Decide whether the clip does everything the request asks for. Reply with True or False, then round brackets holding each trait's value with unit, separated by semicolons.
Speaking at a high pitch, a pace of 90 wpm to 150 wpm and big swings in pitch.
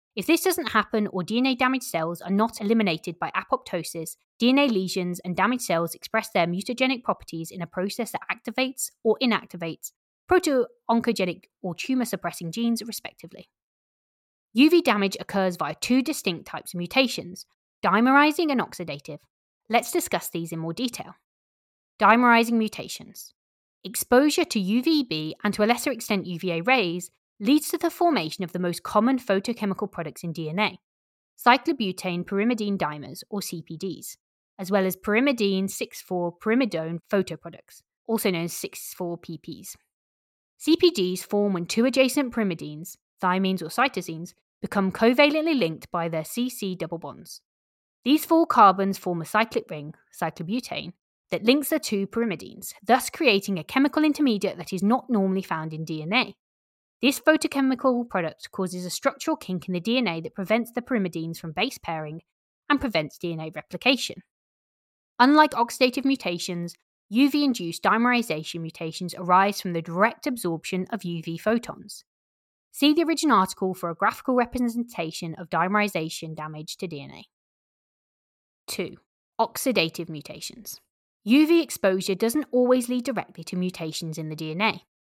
True (200 Hz; 140 wpm; 6.3 semitones)